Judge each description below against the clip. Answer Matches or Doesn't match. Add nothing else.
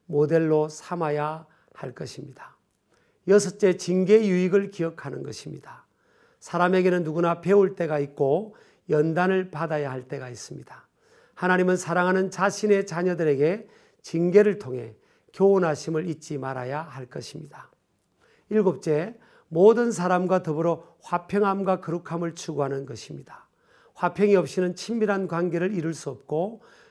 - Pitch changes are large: Doesn't match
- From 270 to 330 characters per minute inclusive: Matches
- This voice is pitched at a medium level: Matches